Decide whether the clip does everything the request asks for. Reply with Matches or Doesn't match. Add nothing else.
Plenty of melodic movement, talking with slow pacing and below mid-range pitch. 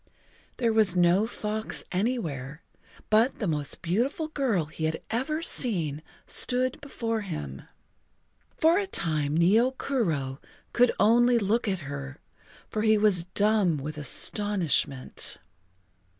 Doesn't match